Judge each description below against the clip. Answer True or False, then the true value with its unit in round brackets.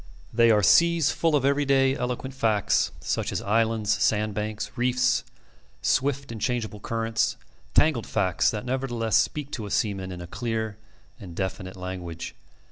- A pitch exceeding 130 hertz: False (115 Hz)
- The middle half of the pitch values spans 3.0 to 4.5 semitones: True (4.0 semitones)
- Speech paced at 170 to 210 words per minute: False (150 wpm)